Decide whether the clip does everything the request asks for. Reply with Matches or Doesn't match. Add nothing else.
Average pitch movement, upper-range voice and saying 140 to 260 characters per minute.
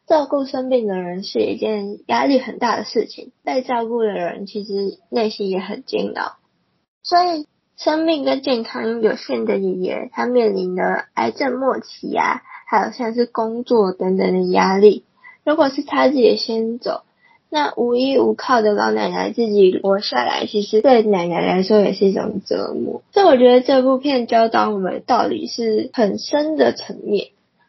Matches